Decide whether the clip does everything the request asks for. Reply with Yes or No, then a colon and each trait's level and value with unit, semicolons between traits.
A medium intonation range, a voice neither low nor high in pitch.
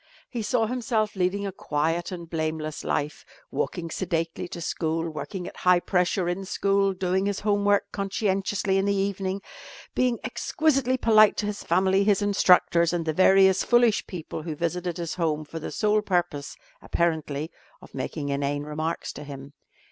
Yes: average, 3.7 semitones; medium, 180 Hz